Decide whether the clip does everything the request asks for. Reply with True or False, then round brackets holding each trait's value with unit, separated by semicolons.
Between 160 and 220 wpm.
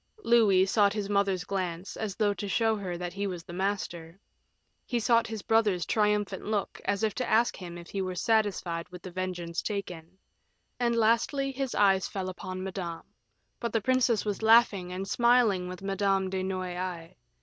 True (175 wpm)